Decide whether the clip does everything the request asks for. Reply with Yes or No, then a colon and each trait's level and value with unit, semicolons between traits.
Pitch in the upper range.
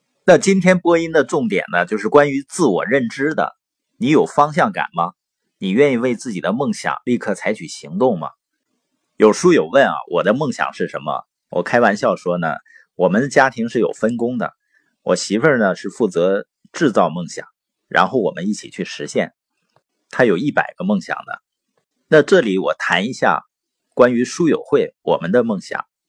No: medium, 145 Hz